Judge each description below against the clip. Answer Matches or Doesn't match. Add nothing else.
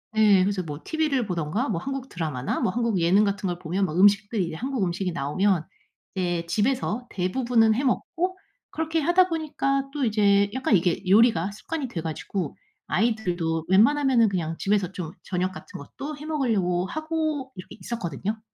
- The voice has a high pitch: Matches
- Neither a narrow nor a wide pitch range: Doesn't match